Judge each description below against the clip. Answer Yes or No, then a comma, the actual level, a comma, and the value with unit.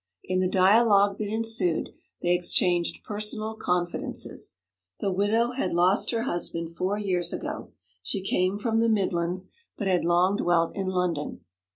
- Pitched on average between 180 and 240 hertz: Yes, medium, 185 Hz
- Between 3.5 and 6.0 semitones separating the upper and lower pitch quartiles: No, average, 3.1 semitones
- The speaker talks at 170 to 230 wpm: No, average, 150 wpm